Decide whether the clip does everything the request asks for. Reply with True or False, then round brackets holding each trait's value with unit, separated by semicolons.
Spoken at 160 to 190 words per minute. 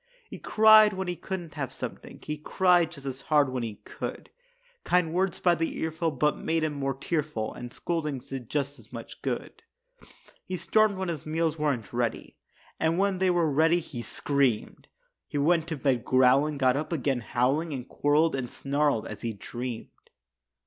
True (180 wpm)